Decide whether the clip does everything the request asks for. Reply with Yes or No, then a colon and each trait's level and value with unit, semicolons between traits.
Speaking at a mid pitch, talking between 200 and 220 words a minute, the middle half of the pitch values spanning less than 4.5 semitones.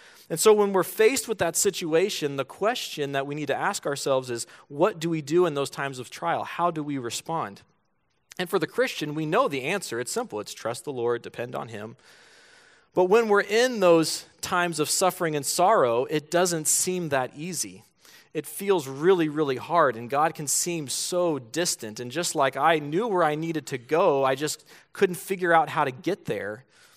Yes: medium, 165 Hz; fast, 205 wpm; average, 3.9 semitones